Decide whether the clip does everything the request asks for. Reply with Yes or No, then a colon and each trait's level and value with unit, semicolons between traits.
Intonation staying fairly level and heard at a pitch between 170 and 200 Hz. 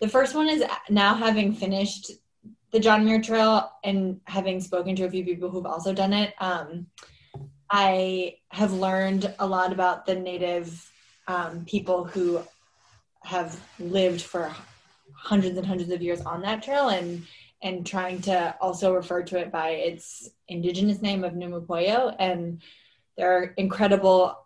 Yes: narrow, 2.2 semitones; medium, 185 Hz